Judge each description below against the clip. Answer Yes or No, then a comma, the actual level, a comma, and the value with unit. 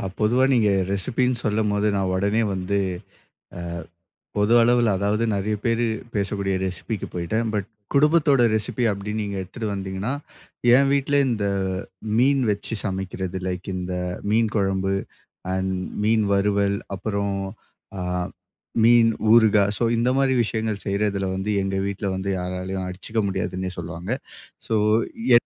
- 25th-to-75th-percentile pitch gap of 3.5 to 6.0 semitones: No, average, 3.0 semitones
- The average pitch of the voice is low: Yes, low, 100 Hz